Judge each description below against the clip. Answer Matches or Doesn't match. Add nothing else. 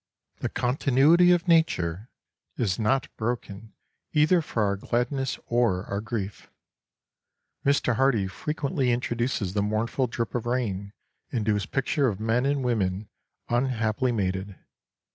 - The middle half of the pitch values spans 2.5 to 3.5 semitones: Doesn't match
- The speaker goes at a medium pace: Doesn't match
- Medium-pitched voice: Doesn't match